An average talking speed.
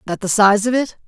No: fast, 280 wpm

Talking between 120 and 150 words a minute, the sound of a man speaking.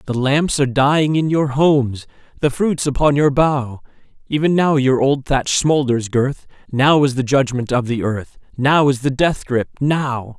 No: average, 185 wpm; male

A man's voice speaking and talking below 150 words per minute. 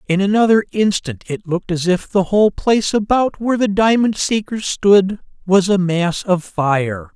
No: male; average, 175 wpm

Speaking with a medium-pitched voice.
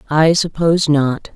Yes: medium, 155 Hz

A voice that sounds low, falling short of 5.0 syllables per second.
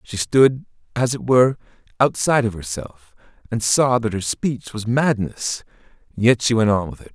Yes: low, 115 Hz; 4.8 syllables/s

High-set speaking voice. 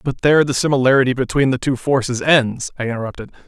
No: low, 130 Hz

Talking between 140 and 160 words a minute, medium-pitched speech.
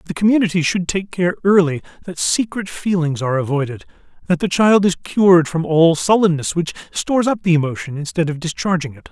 No: average, 185 wpm; medium, 170 Hz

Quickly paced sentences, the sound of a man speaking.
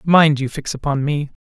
Yes: fast, 210 wpm; male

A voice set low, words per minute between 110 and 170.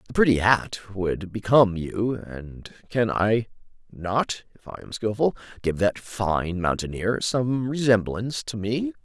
Yes: low, 110 Hz; average, 145 wpm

